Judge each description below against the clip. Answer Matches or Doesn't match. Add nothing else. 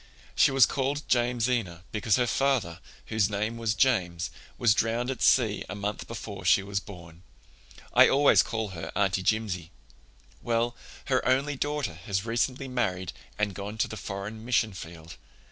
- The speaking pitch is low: Matches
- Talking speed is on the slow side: Doesn't match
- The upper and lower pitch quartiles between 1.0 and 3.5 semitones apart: Doesn't match